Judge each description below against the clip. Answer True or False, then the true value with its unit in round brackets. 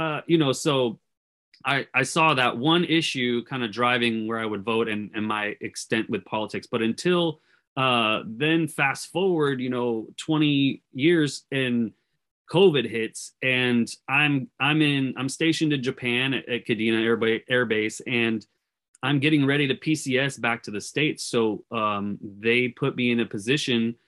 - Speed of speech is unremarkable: True (165 wpm)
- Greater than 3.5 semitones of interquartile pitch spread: True (4.0 semitones)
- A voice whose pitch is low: True (125 Hz)